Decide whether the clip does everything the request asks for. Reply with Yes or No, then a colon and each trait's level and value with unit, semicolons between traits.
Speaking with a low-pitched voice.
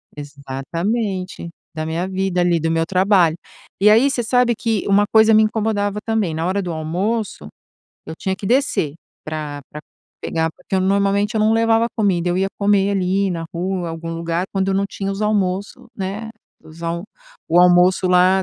No: high, 190 Hz